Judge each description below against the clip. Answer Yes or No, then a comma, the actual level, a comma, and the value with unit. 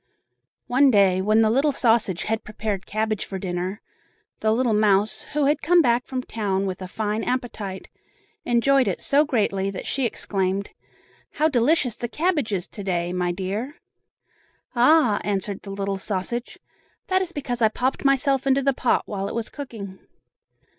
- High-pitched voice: Yes, high, 220 Hz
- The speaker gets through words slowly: No, average, 165 wpm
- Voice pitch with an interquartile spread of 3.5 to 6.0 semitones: Yes, average, 5.1 semitones